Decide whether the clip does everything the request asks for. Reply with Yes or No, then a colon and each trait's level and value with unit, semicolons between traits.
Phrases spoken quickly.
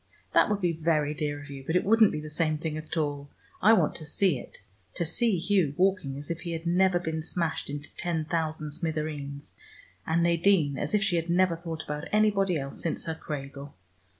Yes: fast, 210 wpm